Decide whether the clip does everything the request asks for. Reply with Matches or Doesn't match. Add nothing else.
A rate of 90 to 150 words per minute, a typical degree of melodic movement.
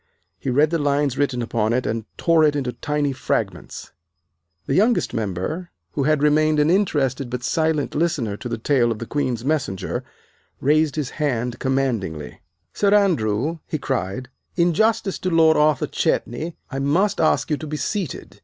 Doesn't match